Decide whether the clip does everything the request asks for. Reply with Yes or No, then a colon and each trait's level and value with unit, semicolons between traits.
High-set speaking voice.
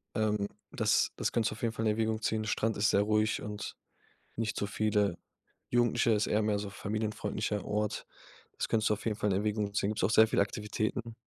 No: low, 105 Hz